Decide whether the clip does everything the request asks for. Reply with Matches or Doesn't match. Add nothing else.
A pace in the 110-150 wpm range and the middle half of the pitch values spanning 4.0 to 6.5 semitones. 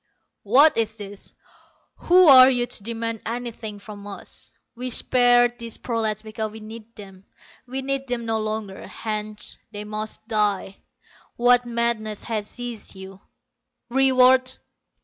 Doesn't match